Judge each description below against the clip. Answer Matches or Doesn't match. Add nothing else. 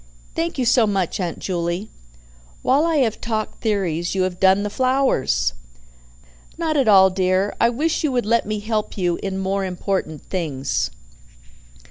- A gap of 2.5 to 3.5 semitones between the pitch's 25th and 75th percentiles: Doesn't match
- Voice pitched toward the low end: Doesn't match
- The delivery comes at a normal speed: Matches